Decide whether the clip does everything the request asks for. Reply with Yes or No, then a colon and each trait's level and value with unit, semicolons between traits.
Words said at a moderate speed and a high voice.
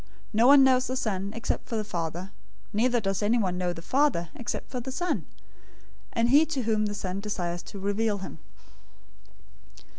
Yes: average, 160 wpm; high, 215 Hz